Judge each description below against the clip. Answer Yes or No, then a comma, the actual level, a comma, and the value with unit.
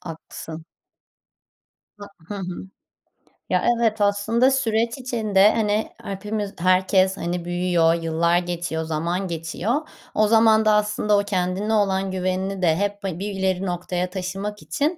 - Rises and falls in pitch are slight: No, average, 3.0 semitones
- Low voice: No, high, 195 Hz